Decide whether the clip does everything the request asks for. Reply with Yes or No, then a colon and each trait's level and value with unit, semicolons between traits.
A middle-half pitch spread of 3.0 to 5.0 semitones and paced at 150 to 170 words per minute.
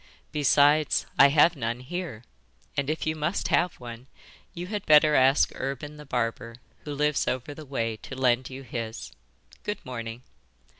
Yes: average, 3.8 semitones; average, 160 wpm